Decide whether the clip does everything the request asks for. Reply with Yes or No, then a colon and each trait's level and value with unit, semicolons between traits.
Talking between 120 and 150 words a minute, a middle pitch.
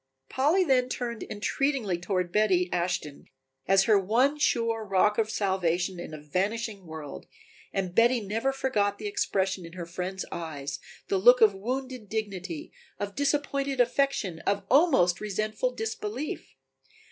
No: average, 140 wpm; high, 205 Hz